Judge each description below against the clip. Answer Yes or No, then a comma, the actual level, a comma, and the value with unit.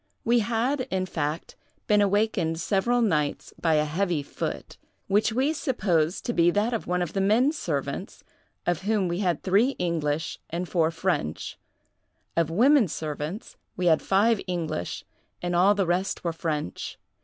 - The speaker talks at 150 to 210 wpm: Yes, average, 160 wpm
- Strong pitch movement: No, average, 4.6 semitones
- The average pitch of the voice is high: No, medium, 180 Hz